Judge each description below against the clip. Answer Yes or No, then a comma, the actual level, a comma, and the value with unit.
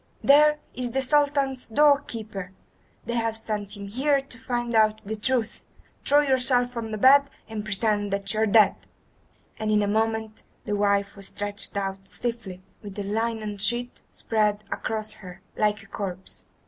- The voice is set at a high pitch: Yes, high, 220 Hz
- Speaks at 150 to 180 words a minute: Yes, average, 175 wpm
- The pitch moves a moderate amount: Yes, average, 3.2 semitones